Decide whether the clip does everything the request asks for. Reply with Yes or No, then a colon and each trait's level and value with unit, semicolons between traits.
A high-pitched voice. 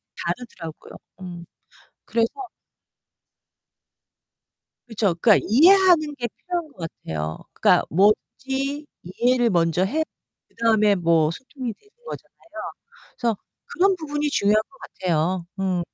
Yes: high, 225 Hz